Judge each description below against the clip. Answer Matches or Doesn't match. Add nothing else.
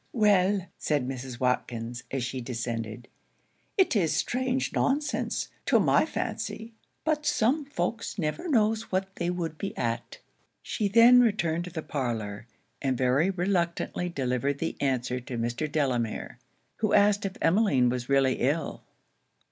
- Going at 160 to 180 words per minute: Doesn't match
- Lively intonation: Matches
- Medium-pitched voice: Matches